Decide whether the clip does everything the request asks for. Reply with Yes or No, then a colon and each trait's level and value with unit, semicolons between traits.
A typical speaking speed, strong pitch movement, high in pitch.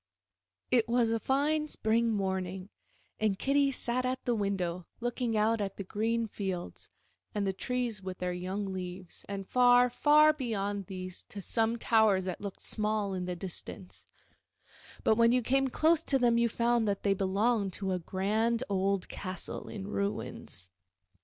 No: average, 165 wpm; average, 3.9 semitones; high, 210 Hz